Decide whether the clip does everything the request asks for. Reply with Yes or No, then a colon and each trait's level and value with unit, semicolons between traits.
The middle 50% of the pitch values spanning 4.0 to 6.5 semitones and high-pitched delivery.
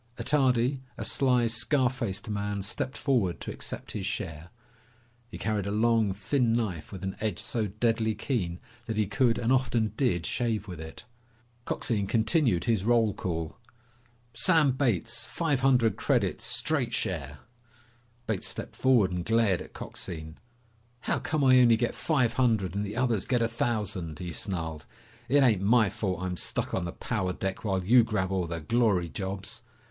No: average, 4.5 semitones; low, 110 Hz